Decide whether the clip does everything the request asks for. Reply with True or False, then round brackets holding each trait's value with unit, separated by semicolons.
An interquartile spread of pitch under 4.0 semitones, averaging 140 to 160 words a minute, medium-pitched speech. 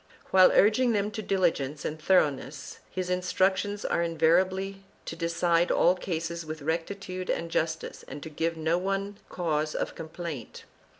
True (3.0 semitones; 155 wpm; 170 Hz)